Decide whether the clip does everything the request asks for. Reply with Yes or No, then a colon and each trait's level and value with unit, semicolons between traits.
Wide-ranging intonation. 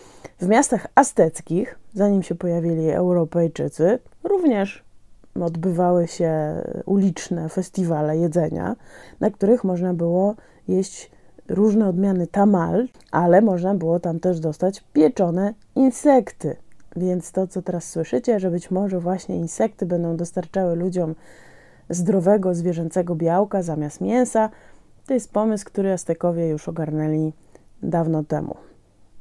No: average, 2.9 semitones